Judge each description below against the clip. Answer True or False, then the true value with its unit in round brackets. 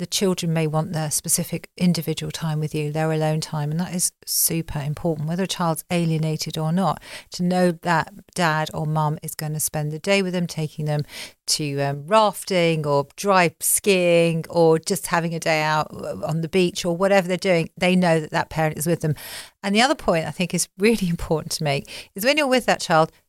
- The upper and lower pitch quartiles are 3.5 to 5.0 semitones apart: False (2.6 semitones)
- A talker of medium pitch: True (165 Hz)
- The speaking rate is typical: False (215 wpm)